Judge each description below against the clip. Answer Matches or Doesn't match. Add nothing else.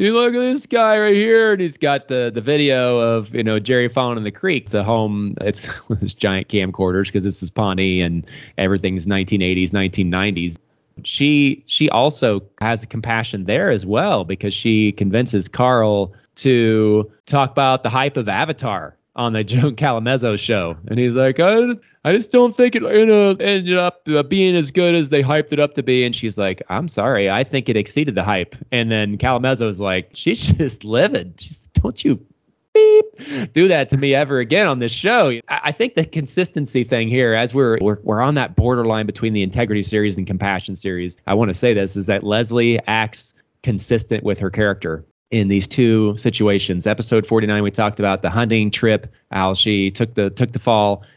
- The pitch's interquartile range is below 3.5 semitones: Doesn't match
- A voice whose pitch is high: Doesn't match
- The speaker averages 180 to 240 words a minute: Matches